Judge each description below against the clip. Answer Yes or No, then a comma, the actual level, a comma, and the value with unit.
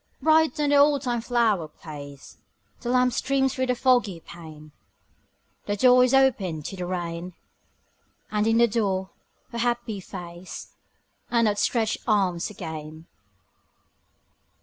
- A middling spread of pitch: No, wide, 6.4 semitones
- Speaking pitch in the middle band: No, high, 215 Hz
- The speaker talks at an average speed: No, slow, 125 wpm